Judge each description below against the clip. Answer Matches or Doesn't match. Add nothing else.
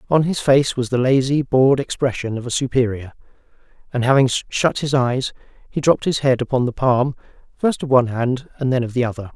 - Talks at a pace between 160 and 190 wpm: Doesn't match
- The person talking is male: Matches